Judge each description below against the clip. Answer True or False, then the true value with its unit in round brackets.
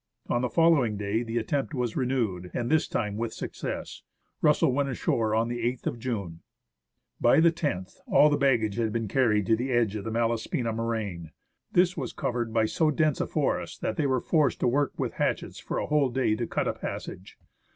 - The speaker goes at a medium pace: False (210 wpm)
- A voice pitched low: True (120 Hz)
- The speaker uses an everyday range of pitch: True (3.6 semitones)